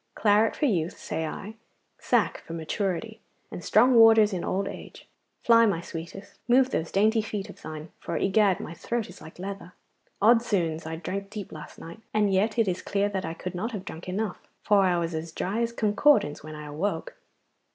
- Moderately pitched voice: No, high, 195 Hz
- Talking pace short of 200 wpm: No, fast, 205 wpm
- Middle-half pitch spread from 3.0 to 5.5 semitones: Yes, average, 4.5 semitones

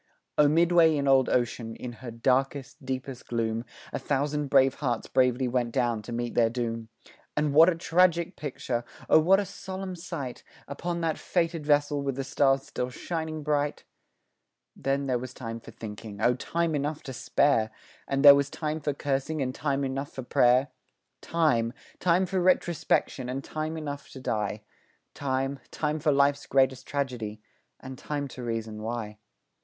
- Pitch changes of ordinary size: Yes, average, 3.8 semitones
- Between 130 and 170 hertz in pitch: Yes, low, 135 Hz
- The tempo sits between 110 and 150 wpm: No, average, 170 wpm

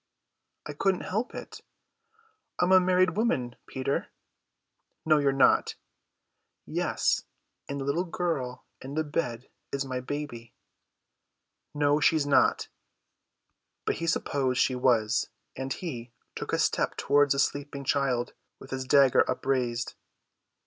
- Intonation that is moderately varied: Yes, average, 3.1 semitones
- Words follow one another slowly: Yes, slow, 130 wpm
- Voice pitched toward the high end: No, medium, 140 Hz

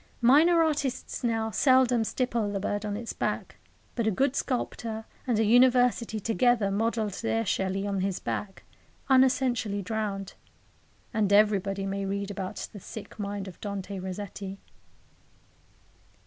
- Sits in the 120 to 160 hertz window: No, high, 215 Hz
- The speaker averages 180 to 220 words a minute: No, slow, 135 wpm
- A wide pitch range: No, average, 3.4 semitones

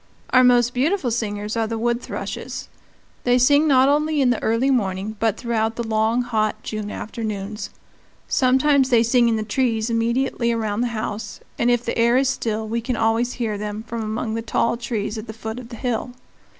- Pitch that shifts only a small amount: Yes, narrow, 2.2 semitones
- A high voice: Yes, high, 230 Hz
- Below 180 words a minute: No, average, 200 wpm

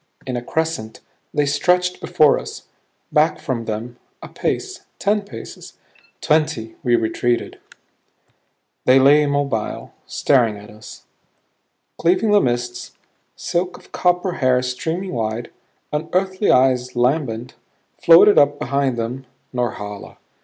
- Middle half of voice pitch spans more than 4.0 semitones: Yes, average, 5.2 semitones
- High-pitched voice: No, low, 130 Hz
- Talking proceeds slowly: Yes, slow, 115 wpm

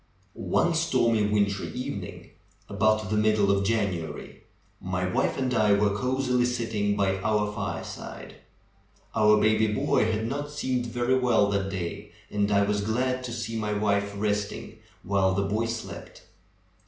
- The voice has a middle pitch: No, low, 105 Hz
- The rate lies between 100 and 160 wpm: Yes, average, 155 wpm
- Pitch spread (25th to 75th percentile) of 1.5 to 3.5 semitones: Yes, narrow, 2.6 semitones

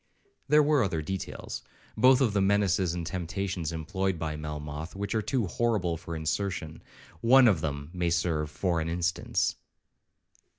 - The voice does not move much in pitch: No, average, 4.0 semitones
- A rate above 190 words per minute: No, average, 155 wpm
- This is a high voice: No, very low, 90 Hz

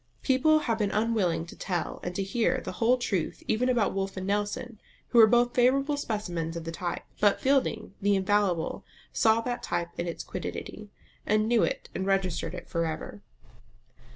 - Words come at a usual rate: Yes, average, 180 wpm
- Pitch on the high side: Yes, high, 205 Hz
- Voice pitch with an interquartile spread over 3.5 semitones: Yes, average, 4.8 semitones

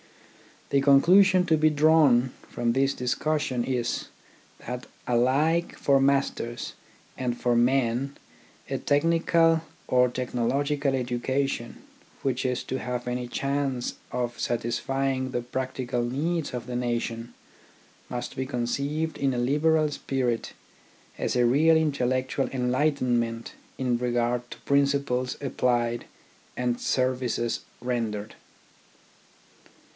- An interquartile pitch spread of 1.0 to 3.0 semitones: Yes, narrow, 2.5 semitones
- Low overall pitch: Yes, low, 130 Hz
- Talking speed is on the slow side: Yes, slow, 110 wpm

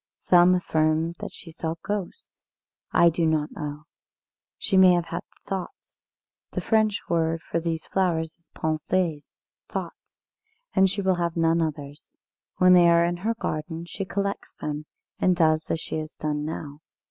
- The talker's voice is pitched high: No, medium, 170 Hz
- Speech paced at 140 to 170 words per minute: Yes, average, 160 wpm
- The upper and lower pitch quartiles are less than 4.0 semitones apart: Yes, narrow, 2.5 semitones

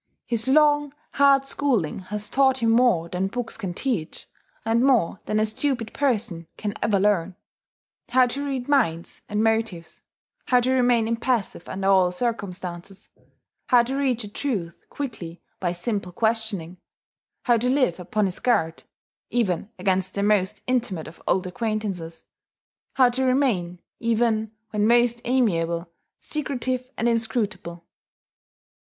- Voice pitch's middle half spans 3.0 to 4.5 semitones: No, average, 5.2 semitones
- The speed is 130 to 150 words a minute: Yes, average, 140 wpm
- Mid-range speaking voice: No, high, 220 Hz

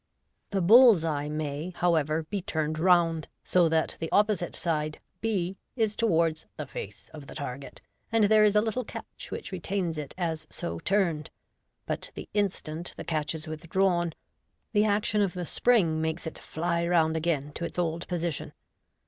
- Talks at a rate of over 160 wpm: Yes, average, 175 wpm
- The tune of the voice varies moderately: Yes, average, 3.7 semitones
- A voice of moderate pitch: Yes, medium, 170 Hz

